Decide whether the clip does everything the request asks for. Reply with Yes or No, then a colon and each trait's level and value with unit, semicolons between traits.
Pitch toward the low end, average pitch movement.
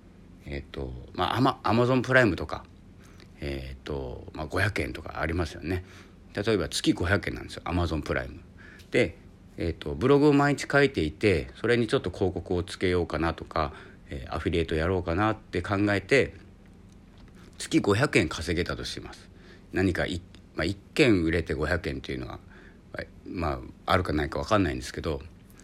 Yes: very low, 90 Hz; average, 3.3 semitones